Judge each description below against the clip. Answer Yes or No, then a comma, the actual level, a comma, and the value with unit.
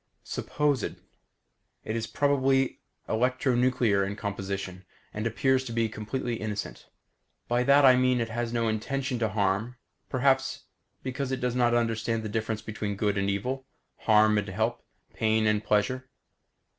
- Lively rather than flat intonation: No, average, 3.3 semitones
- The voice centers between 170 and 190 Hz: No, low, 115 Hz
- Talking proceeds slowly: No, average, 145 wpm